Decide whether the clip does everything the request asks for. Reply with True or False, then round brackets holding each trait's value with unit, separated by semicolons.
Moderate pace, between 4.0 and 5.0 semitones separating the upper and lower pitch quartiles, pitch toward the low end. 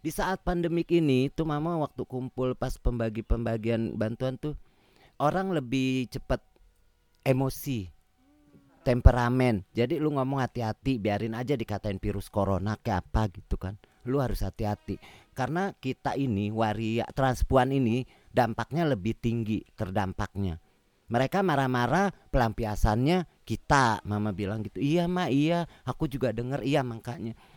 True (125 wpm; 4.4 semitones; 120 Hz)